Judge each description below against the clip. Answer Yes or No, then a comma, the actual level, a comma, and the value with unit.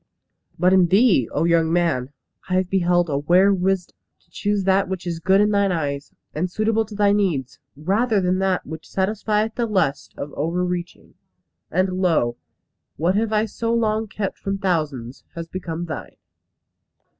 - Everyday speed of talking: Yes, average, 170 wpm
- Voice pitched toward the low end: No, medium, 185 Hz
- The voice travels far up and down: No, average, 3.5 semitones